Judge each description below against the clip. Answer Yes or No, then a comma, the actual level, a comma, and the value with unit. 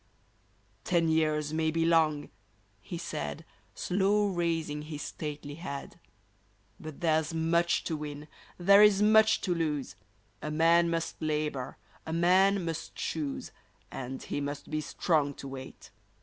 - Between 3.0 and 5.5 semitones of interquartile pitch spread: No, narrow, 2.4 semitones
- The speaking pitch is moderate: Yes, medium, 160 Hz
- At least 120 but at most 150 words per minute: Yes, average, 140 wpm